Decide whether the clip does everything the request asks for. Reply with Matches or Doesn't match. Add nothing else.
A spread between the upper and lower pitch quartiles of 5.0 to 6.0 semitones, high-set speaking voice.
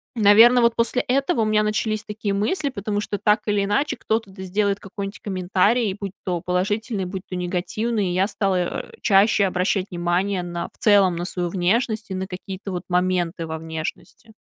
Doesn't match